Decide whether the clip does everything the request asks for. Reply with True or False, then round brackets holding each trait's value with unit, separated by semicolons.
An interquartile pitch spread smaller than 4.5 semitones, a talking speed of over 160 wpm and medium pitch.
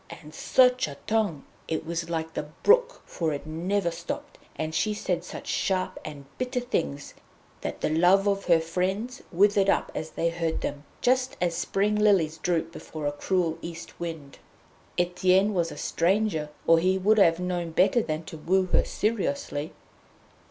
True (4.0 semitones; 170 wpm; 175 Hz)